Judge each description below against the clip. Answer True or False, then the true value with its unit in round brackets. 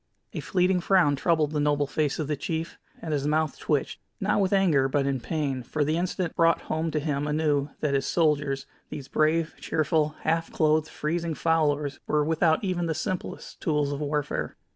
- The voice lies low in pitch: False (155 Hz)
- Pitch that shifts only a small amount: True (2.2 semitones)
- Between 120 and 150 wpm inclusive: False (185 wpm)